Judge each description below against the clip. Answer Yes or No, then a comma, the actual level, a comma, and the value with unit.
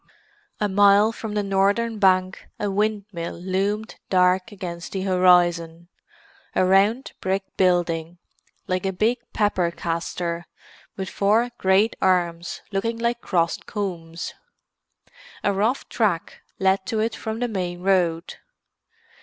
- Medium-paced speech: No, slow, 125 wpm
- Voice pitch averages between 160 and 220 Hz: Yes, high, 190 Hz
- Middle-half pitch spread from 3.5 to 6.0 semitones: No, average, 2.9 semitones